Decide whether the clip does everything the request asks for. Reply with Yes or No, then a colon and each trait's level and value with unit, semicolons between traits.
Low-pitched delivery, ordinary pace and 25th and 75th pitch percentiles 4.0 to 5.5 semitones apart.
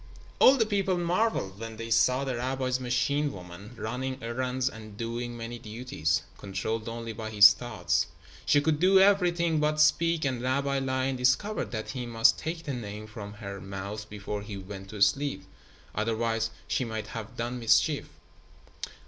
Yes: low, 120 Hz; average, 165 wpm; average, 4.3 semitones